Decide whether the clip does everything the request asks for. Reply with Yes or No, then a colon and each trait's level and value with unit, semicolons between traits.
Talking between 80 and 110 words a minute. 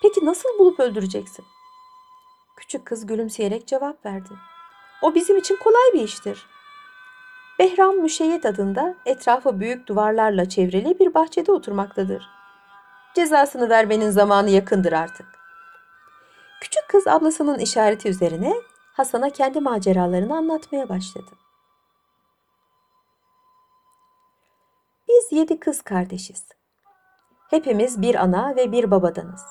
Yes: average, 100 wpm